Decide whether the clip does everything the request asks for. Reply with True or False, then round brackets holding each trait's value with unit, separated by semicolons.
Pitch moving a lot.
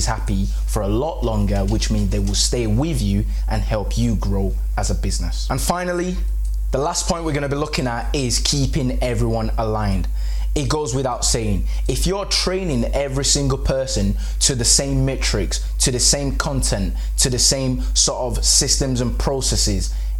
True (5.7 semitones)